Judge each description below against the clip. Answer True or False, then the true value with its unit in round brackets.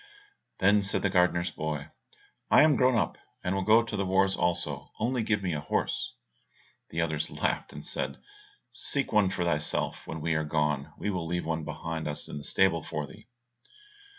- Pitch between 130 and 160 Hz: False (90 Hz)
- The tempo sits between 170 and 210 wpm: True (190 wpm)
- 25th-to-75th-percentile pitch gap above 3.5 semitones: True (4.2 semitones)